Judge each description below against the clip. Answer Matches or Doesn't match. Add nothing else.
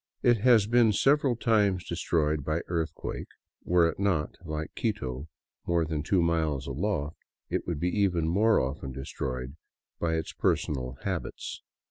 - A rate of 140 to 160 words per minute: Matches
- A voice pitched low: Matches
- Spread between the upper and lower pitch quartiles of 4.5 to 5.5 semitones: Matches